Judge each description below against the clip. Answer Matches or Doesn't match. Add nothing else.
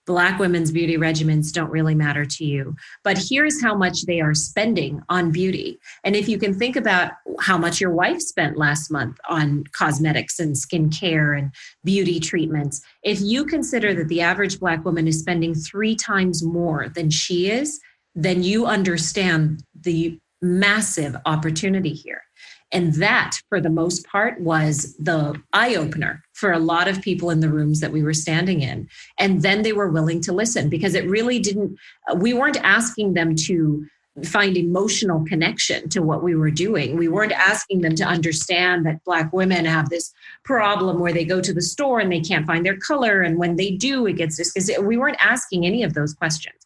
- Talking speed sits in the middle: Matches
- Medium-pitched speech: Matches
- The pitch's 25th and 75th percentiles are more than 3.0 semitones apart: Matches